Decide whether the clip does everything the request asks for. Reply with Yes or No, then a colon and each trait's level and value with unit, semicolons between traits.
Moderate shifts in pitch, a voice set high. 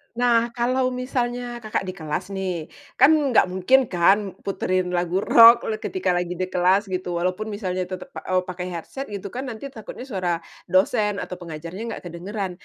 Yes: average, 4.7 semitones; high, 195 Hz